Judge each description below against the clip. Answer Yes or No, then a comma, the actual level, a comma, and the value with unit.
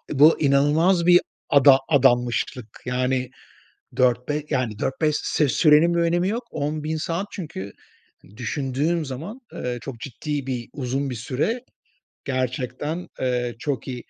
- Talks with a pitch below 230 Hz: Yes, medium, 140 Hz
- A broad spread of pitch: No, average, 3.8 semitones